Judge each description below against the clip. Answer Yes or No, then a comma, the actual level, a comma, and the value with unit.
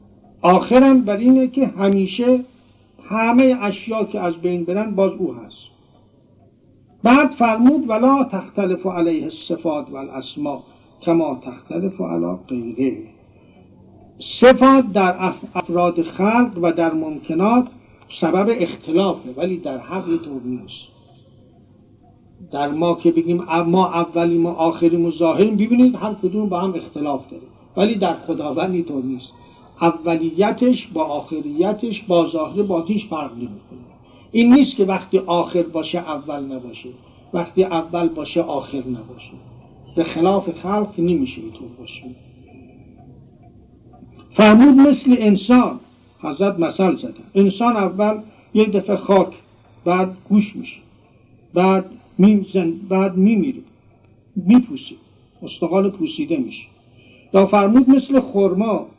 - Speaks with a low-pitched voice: No, medium, 175 Hz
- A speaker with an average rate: Yes, average, 115 wpm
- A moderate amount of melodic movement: No, wide, 6.4 semitones